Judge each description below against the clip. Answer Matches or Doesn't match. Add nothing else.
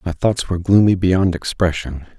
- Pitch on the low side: Matches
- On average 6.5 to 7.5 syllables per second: Doesn't match